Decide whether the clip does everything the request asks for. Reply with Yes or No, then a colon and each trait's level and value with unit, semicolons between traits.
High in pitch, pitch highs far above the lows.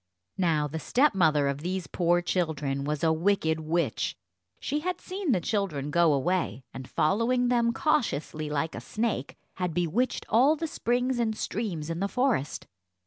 No: medium, 175 Hz; wide, 7.4 semitones